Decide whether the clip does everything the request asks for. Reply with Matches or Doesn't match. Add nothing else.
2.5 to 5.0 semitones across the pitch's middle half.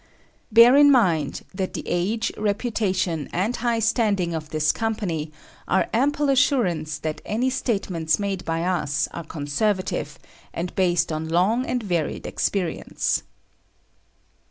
Doesn't match